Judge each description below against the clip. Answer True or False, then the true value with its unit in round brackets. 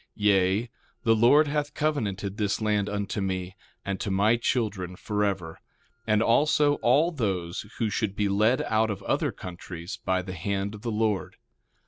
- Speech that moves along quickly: False (160 wpm)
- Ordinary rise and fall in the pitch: True (3.1 semitones)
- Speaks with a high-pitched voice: False (105 Hz)